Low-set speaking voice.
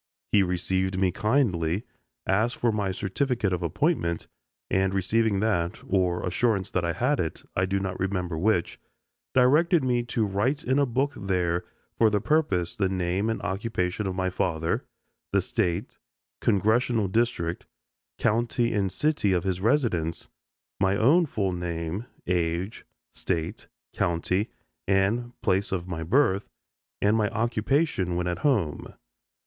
Yes: very low, 95 Hz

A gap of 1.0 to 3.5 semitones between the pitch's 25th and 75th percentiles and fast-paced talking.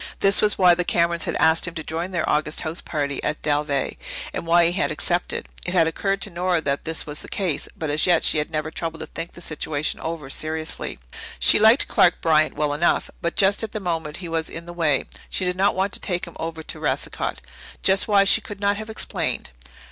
Yes: average, 2.9 semitones; fast, 230 wpm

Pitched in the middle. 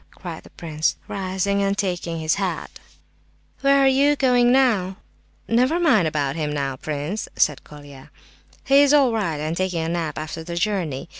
Yes: medium, 180 Hz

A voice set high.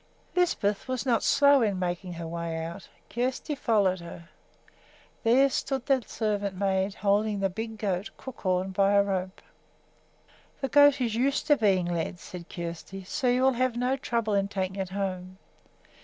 Yes: high, 200 Hz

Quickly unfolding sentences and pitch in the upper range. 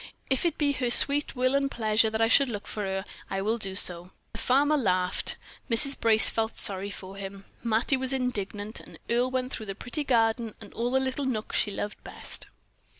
Yes: fast, 210 wpm; high, 225 Hz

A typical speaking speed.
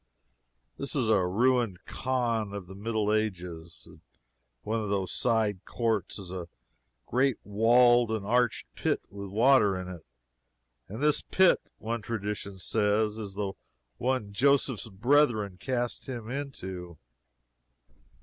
No: slow, 130 wpm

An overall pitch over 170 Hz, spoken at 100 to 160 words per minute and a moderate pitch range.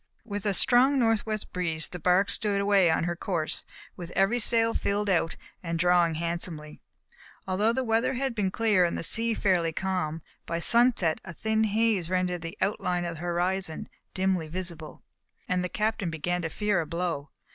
No: medium, 185 Hz; average, 180 wpm; average, 4.0 semitones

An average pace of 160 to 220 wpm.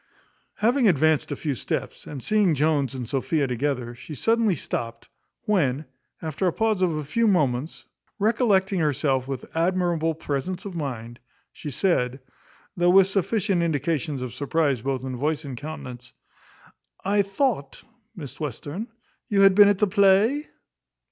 No: average, 150 wpm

